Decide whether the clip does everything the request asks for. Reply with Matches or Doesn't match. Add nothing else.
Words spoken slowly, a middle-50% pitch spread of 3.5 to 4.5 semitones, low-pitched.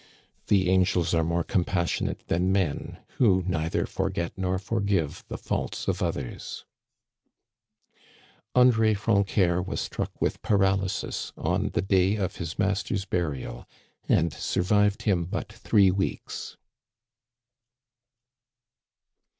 Doesn't match